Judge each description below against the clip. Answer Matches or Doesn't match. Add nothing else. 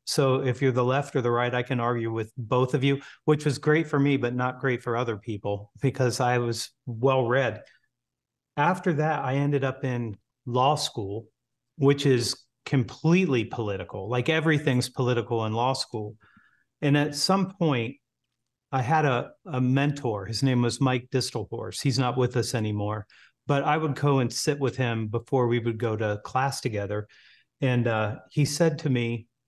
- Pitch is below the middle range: Matches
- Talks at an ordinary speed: Matches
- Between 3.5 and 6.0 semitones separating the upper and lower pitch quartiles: Doesn't match